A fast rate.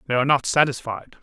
No: average, 195 wpm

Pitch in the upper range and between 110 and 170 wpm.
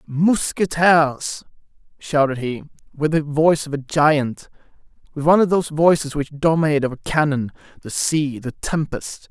No: medium, 150 Hz; average, 140 wpm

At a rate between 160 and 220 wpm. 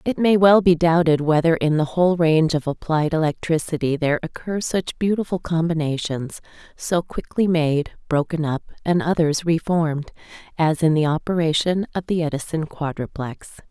No: average, 150 wpm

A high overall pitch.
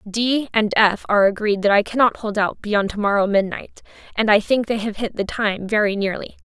Yes: high, 210 Hz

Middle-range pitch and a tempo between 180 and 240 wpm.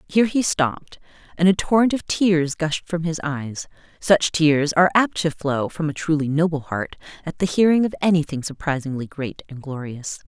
Yes: medium, 160 Hz; average, 185 wpm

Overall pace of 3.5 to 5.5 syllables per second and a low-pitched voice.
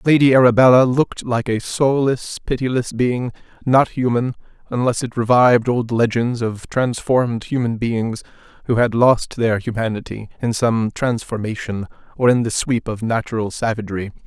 Yes: 4.9 syllables/s; low, 120 Hz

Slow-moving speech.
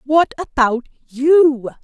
Yes: slow, 100 wpm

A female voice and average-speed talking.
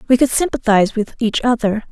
Yes: female; average, 190 wpm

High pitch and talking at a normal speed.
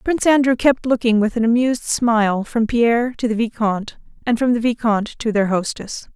Yes: high, 230 Hz; average, 195 wpm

